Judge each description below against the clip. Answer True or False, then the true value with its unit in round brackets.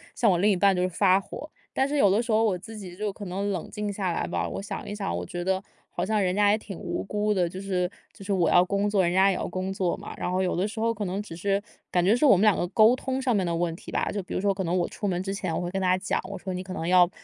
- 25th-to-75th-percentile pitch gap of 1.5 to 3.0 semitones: True (2.4 semitones)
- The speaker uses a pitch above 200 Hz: False (195 Hz)